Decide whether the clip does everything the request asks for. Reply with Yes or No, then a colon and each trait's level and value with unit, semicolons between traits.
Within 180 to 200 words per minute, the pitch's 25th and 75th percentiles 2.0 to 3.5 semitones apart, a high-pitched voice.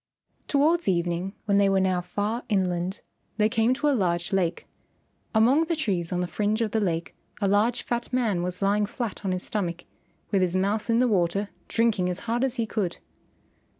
No: average, 195 wpm; average, 4.1 semitones; high, 205 Hz